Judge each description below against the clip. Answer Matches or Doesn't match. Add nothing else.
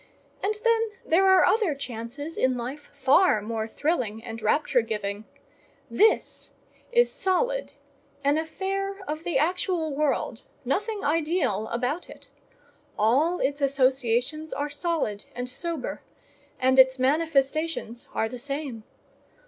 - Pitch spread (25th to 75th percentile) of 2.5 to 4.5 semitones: Doesn't match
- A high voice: Matches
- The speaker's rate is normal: Doesn't match